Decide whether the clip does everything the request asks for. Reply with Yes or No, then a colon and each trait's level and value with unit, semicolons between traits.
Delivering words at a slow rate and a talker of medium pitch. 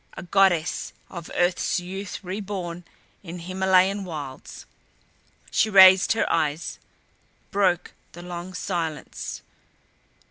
Yes: slow, 100 wpm; medium, 180 Hz